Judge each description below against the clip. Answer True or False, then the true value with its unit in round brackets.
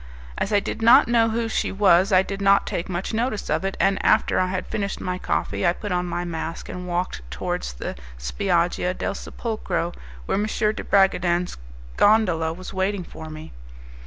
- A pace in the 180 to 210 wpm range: True (190 wpm)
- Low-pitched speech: False (185 Hz)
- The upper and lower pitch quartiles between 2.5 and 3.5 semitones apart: True (2.8 semitones)